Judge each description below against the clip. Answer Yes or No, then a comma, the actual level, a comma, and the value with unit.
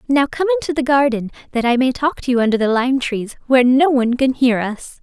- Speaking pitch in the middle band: No, very high, 260 Hz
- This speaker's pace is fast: Yes, fast, 250 wpm